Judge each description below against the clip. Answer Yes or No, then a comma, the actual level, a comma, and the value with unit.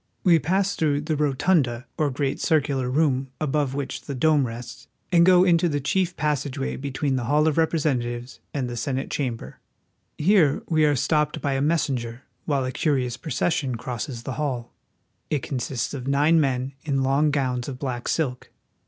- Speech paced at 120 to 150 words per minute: No, average, 180 wpm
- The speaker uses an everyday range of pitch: Yes, average, 3.1 semitones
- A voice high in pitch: No, medium, 140 Hz